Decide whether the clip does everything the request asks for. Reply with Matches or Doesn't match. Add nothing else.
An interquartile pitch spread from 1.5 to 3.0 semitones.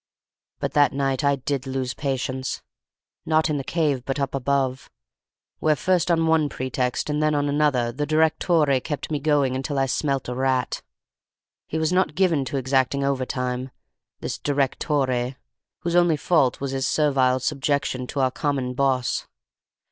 Matches